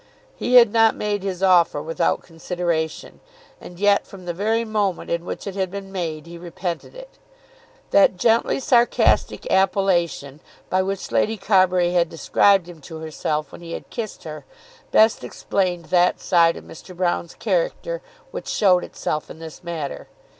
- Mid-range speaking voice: Yes, medium, 180 Hz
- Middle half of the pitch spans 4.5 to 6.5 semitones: No, average, 3.3 semitones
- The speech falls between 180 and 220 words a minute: No, average, 160 wpm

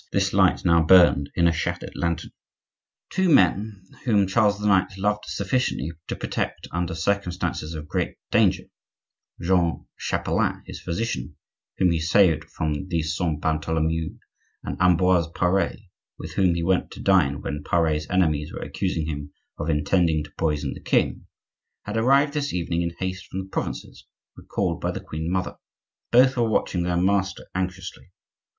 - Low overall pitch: Yes, very low, 90 Hz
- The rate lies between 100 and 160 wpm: Yes, average, 150 wpm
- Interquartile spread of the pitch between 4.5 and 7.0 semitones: No, average, 3.1 semitones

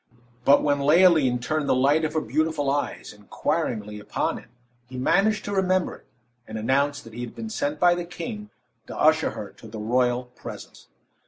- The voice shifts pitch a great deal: Yes, wide, 6.1 semitones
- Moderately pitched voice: Yes, medium, 145 Hz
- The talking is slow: No, average, 185 wpm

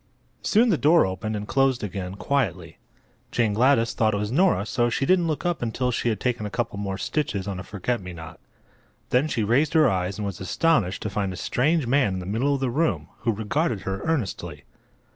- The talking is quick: Yes, fast, 220 wpm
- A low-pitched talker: Yes, low, 115 Hz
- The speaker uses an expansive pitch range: Yes, wide, 6.0 semitones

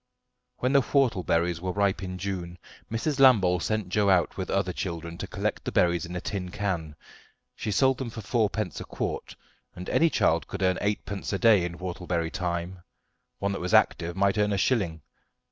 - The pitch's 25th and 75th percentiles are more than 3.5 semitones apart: No, average, 3.2 semitones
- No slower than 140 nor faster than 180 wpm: No, average, 190 wpm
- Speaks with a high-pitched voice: No, very low, 95 Hz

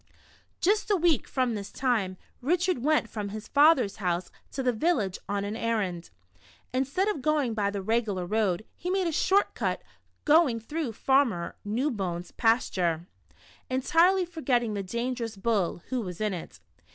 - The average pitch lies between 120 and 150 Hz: No, high, 235 Hz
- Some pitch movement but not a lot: No, wide, 7.0 semitones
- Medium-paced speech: Yes, average, 155 wpm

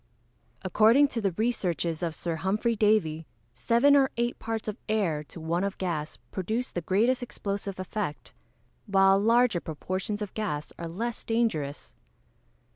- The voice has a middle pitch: No, high, 200 Hz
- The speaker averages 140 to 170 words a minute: Yes, average, 150 wpm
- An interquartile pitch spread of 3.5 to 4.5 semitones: No, average, 5.0 semitones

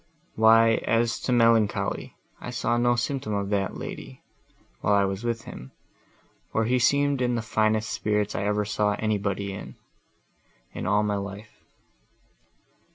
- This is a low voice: Yes, low, 110 Hz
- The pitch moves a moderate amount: No, narrow, 2.3 semitones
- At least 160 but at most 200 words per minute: No, average, 150 wpm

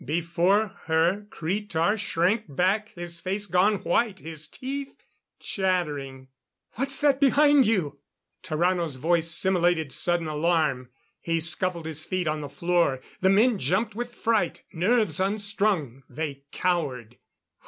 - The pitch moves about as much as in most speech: Yes, average, 4.6 semitones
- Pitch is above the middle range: No, medium, 175 Hz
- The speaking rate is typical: No, slow, 125 wpm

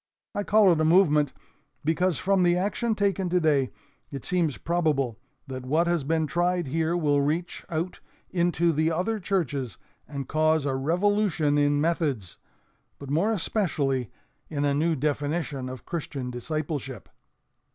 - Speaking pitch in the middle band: Yes, medium, 155 Hz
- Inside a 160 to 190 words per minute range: No, average, 145 wpm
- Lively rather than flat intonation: No, average, 3.7 semitones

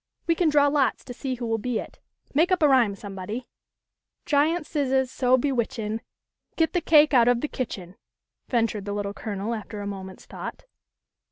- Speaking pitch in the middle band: No, high, 245 Hz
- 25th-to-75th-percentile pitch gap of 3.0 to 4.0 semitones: No, wide, 5.5 semitones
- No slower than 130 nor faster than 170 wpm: No, average, 190 wpm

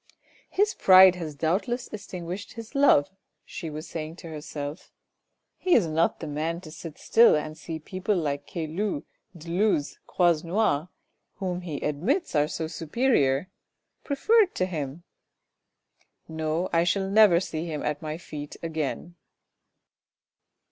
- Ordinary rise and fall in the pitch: Yes, average, 3.9 semitones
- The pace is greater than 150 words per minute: No, average, 145 wpm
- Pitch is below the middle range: No, medium, 165 Hz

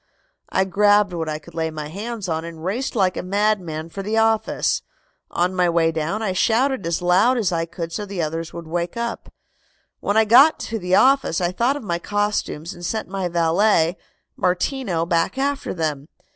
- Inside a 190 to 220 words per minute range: Yes, average, 195 wpm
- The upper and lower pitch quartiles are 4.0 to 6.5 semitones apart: Yes, average, 4.4 semitones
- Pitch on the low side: No, medium, 185 Hz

